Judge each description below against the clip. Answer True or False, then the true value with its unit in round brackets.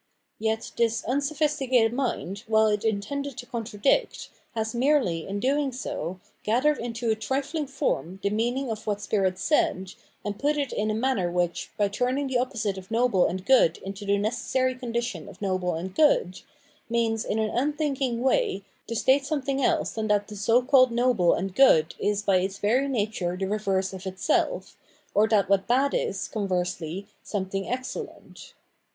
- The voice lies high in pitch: True (220 Hz)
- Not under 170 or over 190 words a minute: True (175 wpm)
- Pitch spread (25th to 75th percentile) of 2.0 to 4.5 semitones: False (4.9 semitones)